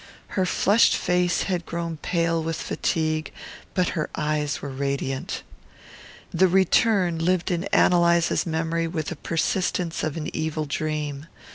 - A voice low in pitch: No, medium, 165 Hz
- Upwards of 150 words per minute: No, average, 140 wpm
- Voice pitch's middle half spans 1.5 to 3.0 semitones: Yes, narrow, 2.4 semitones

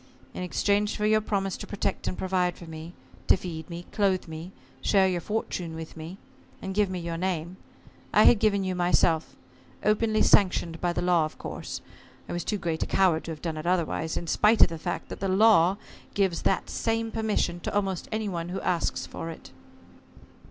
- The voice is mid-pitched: Yes, medium, 180 Hz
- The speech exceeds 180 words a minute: Yes, average, 200 wpm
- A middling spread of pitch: Yes, average, 3.2 semitones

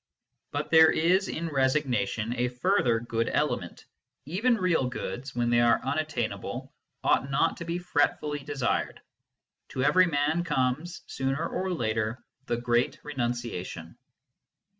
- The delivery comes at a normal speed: No, slow, 130 wpm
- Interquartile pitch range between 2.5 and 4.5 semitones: No, average, 5.2 semitones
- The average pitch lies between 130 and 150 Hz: Yes, low, 135 Hz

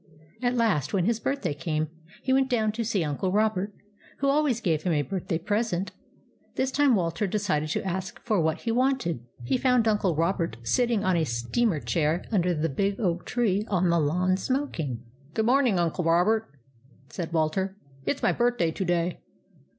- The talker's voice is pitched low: No, high, 190 Hz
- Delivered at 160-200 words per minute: Yes, average, 190 wpm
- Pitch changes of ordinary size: No, wide, 5.7 semitones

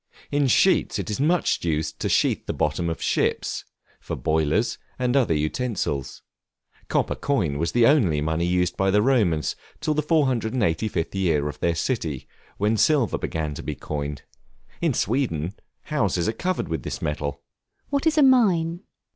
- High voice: No, very low, 95 Hz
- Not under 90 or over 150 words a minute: No, average, 165 wpm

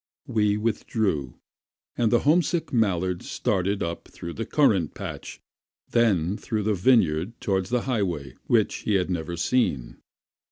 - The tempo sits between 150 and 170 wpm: No, slow, 135 wpm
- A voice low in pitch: Yes, low, 100 Hz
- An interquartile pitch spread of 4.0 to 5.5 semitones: Yes, average, 5.0 semitones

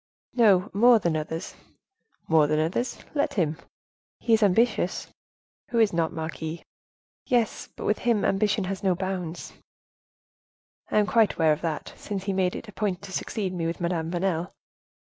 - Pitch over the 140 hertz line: Yes, medium, 185 Hz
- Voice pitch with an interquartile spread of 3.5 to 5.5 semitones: Yes, average, 4.2 semitones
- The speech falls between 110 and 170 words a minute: Yes, average, 160 wpm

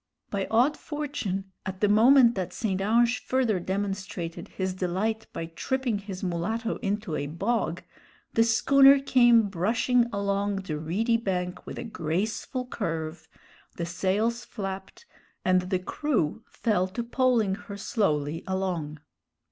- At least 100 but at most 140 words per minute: Yes, slow, 135 wpm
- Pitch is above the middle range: Yes, high, 200 Hz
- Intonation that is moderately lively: Yes, average, 4.2 semitones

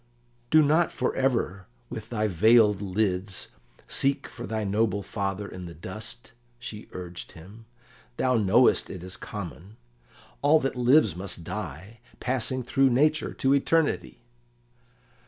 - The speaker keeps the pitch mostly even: No, average, 5.1 semitones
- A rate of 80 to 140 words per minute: Yes, slow, 135 wpm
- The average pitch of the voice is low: Yes, low, 110 Hz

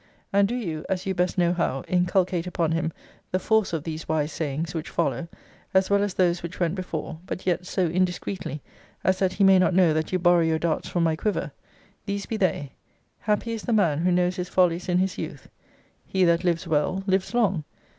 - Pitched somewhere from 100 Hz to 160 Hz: No, medium, 180 Hz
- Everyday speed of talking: No, fast, 215 wpm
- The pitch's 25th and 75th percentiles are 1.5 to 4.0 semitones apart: Yes, narrow, 2.4 semitones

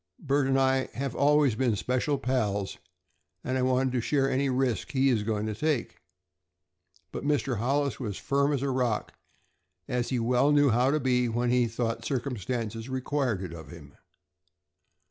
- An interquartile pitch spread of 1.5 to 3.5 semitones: Yes, average, 2.9 semitones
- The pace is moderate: Yes, average, 170 wpm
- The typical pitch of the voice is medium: No, low, 130 Hz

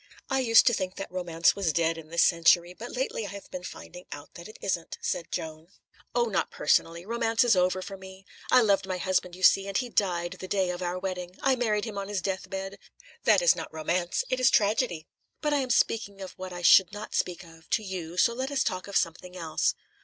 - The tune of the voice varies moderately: Yes, average, 3.4 semitones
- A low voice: No, high, 190 Hz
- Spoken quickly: Yes, fast, 235 wpm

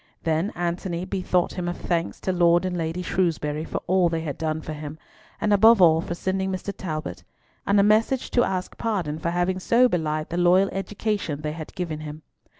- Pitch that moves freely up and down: No, average, 3.2 semitones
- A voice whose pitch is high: No, medium, 175 Hz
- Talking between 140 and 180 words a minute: No, average, 200 wpm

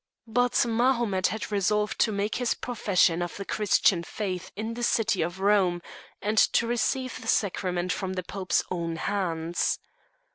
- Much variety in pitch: No, average, 3.7 semitones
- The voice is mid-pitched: No, high, 200 Hz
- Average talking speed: Yes, average, 155 wpm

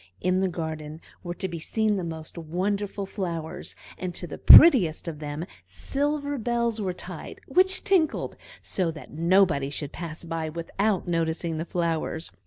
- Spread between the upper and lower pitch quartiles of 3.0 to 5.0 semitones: Yes, average, 4.1 semitones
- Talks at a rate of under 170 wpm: Yes, average, 160 wpm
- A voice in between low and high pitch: Yes, medium, 175 Hz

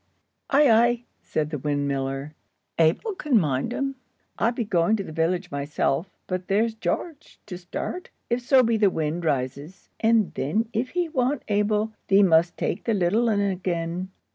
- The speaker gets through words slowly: No, average, 165 wpm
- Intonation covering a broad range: Yes, wide, 6.2 semitones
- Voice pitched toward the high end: Yes, high, 195 Hz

